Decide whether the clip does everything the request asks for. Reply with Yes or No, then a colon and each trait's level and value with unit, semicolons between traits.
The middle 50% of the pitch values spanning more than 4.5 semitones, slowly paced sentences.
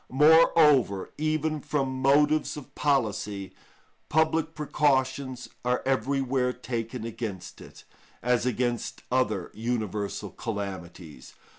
Yes: average, 5.1 semitones; slow, 95 wpm